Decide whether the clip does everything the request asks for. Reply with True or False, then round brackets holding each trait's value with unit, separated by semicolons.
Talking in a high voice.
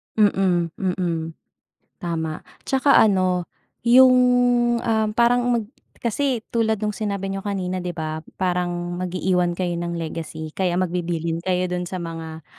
False (180 Hz)